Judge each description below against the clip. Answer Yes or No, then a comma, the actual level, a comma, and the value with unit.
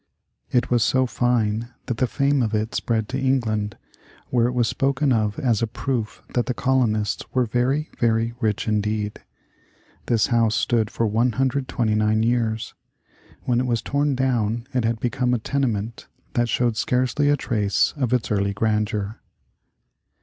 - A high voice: No, low, 120 Hz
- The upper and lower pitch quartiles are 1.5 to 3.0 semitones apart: Yes, average, 2.7 semitones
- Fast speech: No, average, 155 wpm